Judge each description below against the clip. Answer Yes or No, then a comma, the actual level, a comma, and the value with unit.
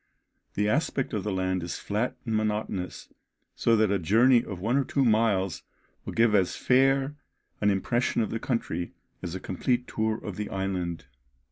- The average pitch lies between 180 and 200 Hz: No, low, 105 Hz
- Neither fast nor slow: Yes, average, 175 wpm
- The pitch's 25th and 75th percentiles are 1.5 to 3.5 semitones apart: No, average, 3.9 semitones